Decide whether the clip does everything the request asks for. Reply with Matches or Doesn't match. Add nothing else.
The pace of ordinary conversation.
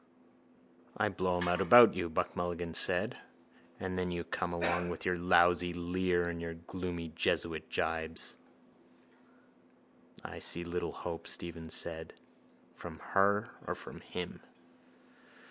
Doesn't match